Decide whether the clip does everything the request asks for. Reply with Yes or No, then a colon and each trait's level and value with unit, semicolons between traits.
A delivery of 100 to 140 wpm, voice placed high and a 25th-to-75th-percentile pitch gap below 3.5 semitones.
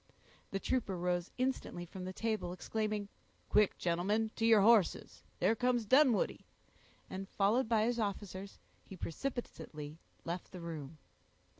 No: slow, 135 wpm; high, 205 Hz; average, 4.0 semitones